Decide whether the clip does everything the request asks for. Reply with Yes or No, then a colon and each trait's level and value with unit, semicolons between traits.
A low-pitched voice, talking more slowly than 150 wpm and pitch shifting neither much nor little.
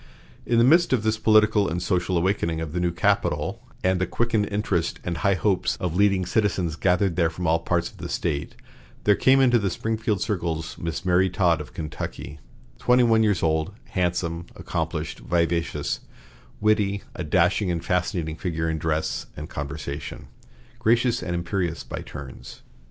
No: very low, 90 Hz; average, 170 wpm; average, 3.8 semitones